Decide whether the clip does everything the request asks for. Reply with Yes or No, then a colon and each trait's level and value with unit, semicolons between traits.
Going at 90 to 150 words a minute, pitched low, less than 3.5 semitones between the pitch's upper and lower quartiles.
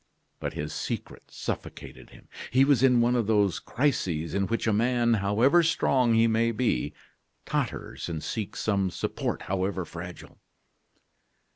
No: average, 145 wpm; low, 110 Hz; average, 4.3 semitones